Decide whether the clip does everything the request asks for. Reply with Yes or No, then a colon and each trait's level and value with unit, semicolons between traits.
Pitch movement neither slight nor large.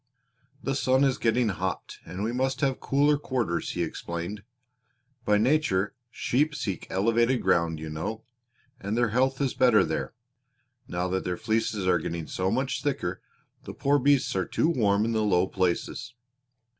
No: wide, 5.9 semitones